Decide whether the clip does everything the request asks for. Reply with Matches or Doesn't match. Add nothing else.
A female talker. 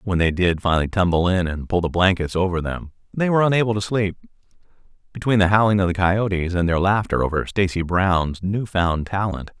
Doesn't match